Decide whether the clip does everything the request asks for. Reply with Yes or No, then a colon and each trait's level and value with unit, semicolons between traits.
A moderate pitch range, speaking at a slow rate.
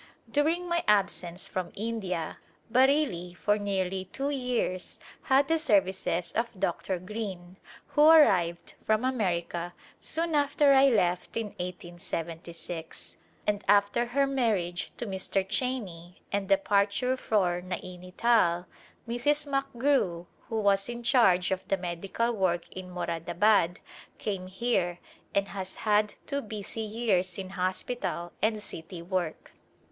Yes: average, 5.0 semitones; slow, 125 wpm